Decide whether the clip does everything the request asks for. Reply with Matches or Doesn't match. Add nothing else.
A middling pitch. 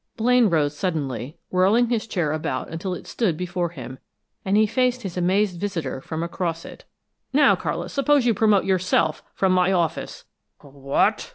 Matches